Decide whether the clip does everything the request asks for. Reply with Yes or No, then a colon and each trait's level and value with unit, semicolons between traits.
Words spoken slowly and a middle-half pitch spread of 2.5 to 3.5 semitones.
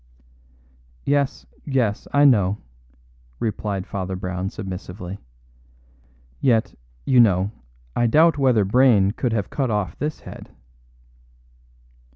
No: slow, 105 wpm; average, 5.3 semitones